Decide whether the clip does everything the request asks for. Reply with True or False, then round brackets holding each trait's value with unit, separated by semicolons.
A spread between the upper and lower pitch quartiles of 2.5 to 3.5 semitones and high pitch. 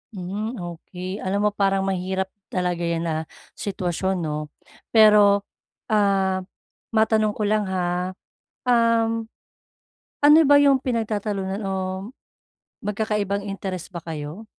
True (2.8 semitones; 195 Hz)